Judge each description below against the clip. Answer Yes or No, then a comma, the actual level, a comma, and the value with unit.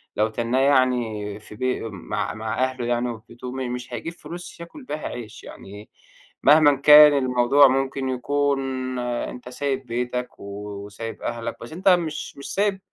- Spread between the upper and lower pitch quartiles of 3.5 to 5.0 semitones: No, average, 3.1 semitones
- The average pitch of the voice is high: No, low, 130 Hz